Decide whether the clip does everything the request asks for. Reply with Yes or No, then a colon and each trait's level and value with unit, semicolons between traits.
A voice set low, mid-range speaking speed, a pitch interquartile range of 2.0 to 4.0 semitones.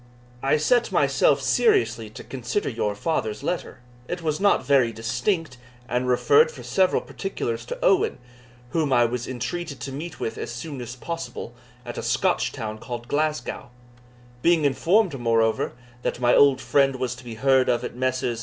No: low, 130 Hz; average, 170 wpm; average, 5.2 semitones